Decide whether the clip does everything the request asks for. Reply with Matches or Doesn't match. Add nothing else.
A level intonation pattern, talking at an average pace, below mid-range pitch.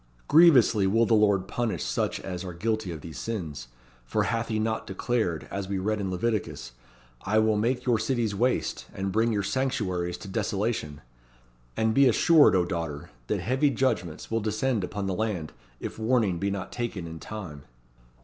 Doesn't match